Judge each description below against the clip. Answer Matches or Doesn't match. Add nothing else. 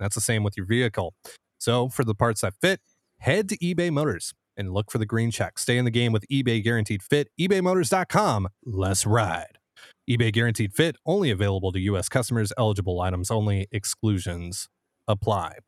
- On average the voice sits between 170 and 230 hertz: Doesn't match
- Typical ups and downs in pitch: Matches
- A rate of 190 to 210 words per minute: Doesn't match